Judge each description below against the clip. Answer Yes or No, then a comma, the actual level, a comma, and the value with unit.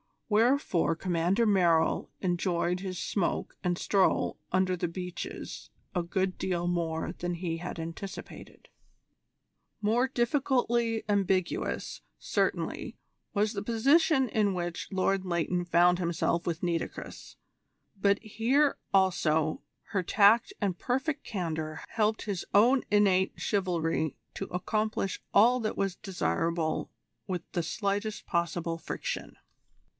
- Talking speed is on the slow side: Yes, slow, 115 wpm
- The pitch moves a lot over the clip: No, average, 3.8 semitones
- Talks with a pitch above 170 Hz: Yes, medium, 185 Hz